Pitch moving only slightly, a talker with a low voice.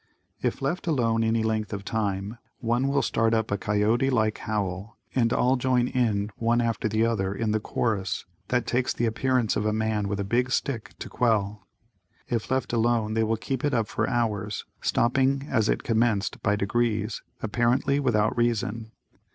Yes: narrow, 2.3 semitones; low, 115 Hz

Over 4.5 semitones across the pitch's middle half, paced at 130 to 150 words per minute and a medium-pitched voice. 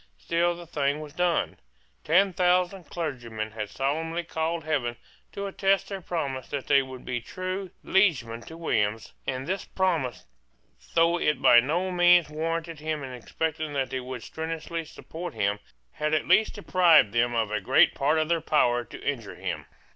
No: average, 5.1 semitones; average, 170 wpm; medium, 155 Hz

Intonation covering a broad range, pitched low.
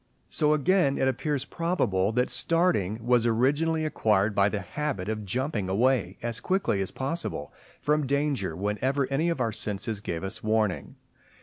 Yes: wide, 6.3 semitones; low, 125 Hz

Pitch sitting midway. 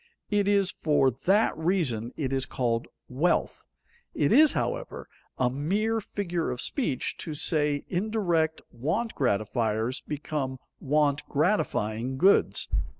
Yes: medium, 150 Hz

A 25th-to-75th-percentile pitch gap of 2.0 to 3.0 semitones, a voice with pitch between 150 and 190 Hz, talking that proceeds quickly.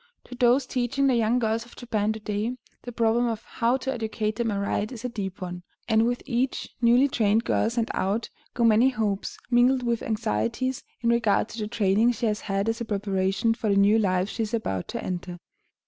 No: narrow, 2.6 semitones; high, 225 Hz; fast, 210 wpm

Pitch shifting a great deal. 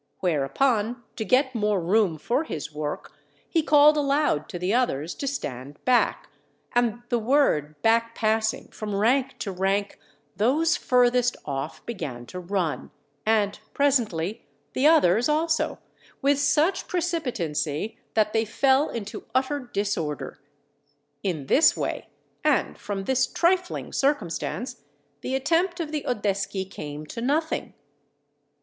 Yes: wide, 7.0 semitones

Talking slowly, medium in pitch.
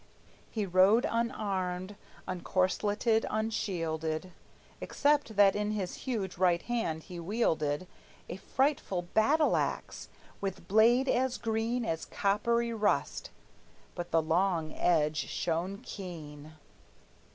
No: slow, 105 wpm; high, 195 Hz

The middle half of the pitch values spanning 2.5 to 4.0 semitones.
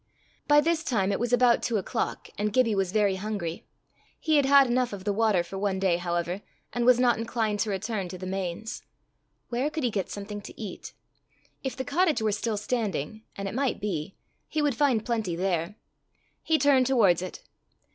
No: average, 4.5 semitones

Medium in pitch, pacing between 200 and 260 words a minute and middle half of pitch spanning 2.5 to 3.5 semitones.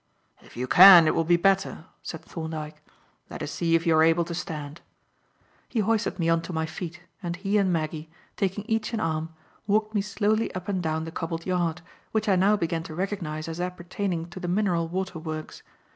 Yes: medium, 175 Hz; fast, 205 wpm; average, 3.2 semitones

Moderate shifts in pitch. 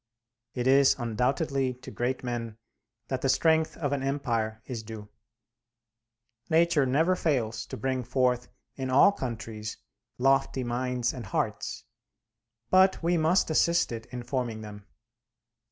Yes: average, 3.4 semitones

